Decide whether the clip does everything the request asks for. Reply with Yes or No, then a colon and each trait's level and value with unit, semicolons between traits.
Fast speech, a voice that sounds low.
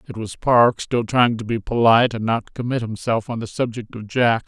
Yes: fast, 230 wpm; low, 115 Hz